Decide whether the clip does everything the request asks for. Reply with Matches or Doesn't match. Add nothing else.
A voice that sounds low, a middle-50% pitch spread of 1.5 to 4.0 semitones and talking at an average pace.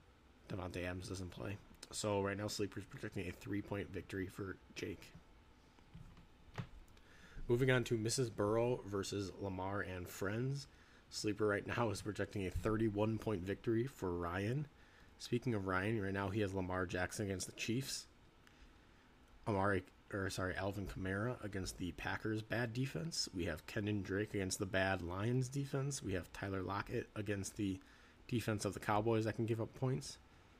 Matches